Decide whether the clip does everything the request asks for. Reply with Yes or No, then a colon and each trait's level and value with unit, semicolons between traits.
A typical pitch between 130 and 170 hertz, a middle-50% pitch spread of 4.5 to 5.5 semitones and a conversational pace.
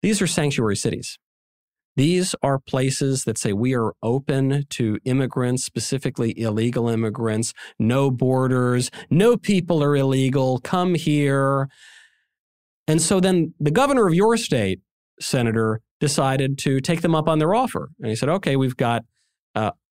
Yes: low, 135 Hz; average, 5.1 semitones; average, 150 wpm